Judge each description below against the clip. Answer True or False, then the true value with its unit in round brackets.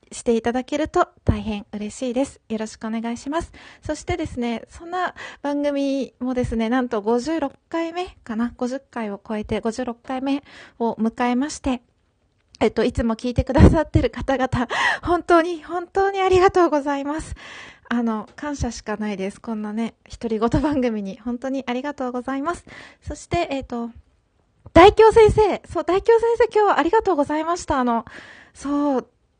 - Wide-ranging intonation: True (5.9 semitones)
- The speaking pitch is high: True (265 Hz)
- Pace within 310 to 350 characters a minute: True (330 characters per minute)